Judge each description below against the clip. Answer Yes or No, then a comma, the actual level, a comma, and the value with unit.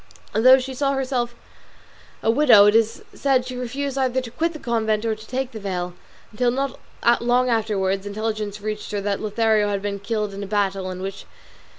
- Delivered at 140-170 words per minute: No, average, 195 wpm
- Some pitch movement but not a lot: Yes, average, 3.7 semitones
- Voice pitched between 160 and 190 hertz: No, high, 225 Hz